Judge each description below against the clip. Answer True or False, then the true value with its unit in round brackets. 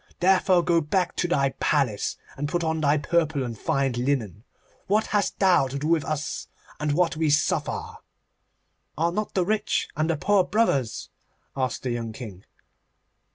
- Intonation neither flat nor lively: True (4.6 semitones)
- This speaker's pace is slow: False (165 wpm)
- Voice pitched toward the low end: False (155 Hz)